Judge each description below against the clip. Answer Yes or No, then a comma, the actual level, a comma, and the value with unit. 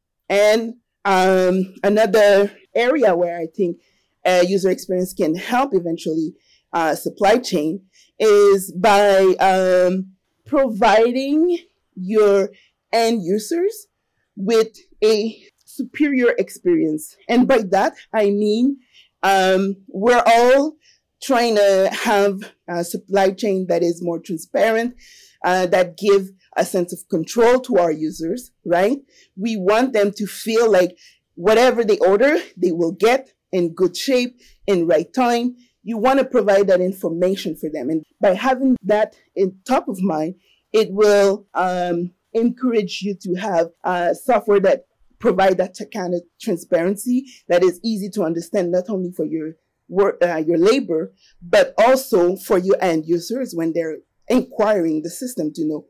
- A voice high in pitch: Yes, high, 200 Hz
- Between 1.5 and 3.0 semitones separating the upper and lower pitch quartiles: No, average, 4.5 semitones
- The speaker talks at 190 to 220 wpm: No, average, 140 wpm